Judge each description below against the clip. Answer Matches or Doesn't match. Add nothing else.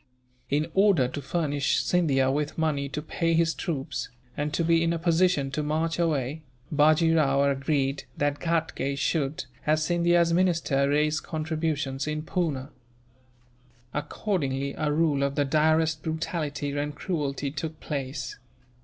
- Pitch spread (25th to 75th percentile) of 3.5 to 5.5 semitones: Doesn't match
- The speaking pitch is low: Doesn't match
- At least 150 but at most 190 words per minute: Doesn't match